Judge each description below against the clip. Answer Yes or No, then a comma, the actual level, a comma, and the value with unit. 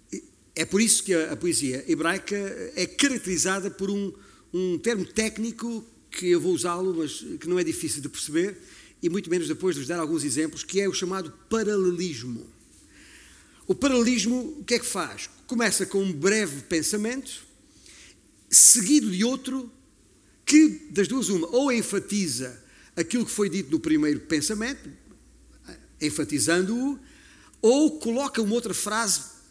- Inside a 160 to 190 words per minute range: No, average, 150 wpm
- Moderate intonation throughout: No, wide, 5.8 semitones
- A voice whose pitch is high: Yes, high, 195 Hz